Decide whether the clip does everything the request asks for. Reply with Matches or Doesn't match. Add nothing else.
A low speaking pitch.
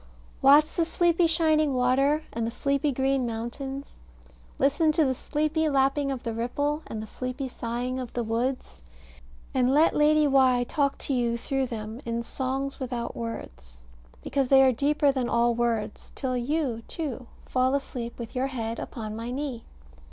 Doesn't match